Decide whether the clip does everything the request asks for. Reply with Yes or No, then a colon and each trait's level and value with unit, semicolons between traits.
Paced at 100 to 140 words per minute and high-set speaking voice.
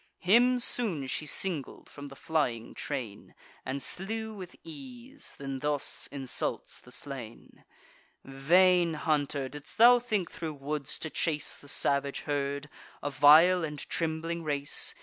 No: slow, 135 wpm; medium, 150 Hz